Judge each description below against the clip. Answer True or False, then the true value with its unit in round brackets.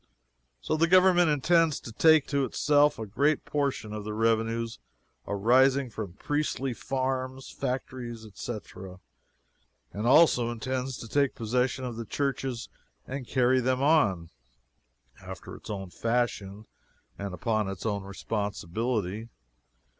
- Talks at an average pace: False (125 wpm)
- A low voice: True (120 Hz)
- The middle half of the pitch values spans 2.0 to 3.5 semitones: False (4.1 semitones)